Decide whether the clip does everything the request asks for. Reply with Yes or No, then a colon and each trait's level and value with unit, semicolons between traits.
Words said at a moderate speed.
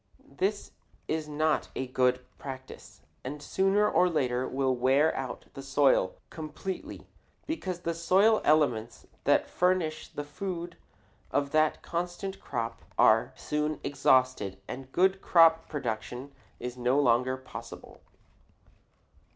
No: slow, 120 wpm